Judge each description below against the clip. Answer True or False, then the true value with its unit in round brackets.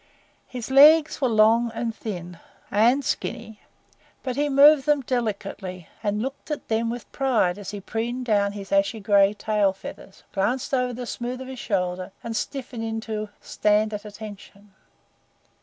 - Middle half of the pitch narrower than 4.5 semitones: True (3.6 semitones)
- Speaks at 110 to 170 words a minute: True (155 wpm)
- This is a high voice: True (225 Hz)